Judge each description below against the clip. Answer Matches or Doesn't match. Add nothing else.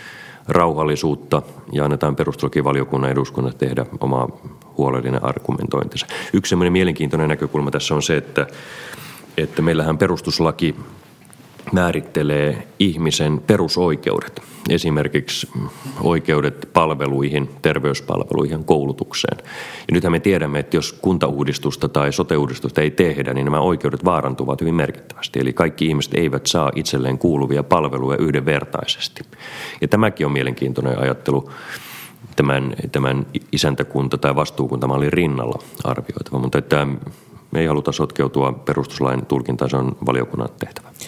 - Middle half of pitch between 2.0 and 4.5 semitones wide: Matches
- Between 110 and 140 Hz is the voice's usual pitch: Doesn't match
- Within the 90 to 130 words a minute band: Matches